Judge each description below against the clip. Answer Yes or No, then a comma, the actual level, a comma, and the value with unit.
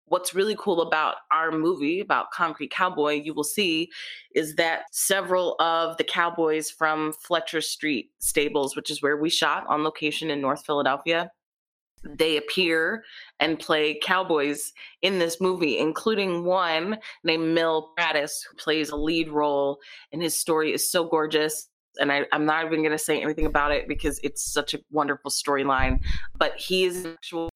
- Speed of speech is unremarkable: Yes, average, 170 wpm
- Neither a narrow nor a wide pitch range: No, narrow, 2.3 semitones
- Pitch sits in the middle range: Yes, medium, 155 Hz